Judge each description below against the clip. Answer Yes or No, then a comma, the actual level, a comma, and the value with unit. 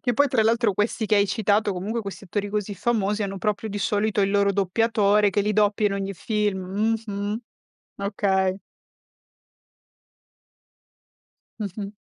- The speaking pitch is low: No, high, 205 Hz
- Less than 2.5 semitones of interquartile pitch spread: Yes, narrow, 1.3 semitones